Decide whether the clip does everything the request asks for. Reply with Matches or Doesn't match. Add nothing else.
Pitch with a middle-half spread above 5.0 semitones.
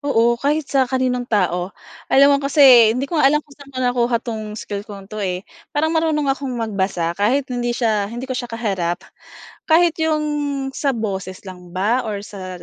Matches